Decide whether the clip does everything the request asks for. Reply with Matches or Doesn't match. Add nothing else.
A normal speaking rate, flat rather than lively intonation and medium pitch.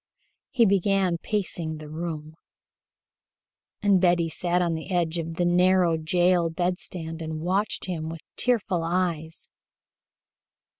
Doesn't match